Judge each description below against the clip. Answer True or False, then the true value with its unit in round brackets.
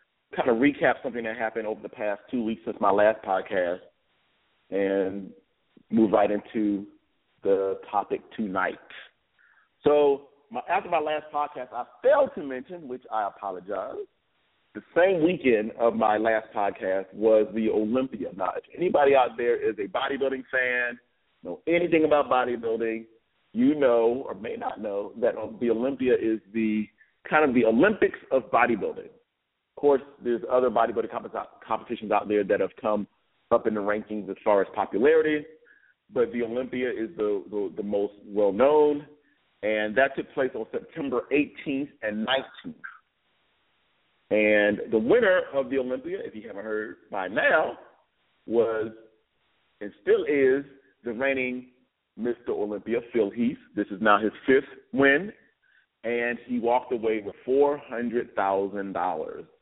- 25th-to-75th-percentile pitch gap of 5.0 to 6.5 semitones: True (5.3 semitones)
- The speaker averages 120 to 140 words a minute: False (150 wpm)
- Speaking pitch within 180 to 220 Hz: False (125 Hz)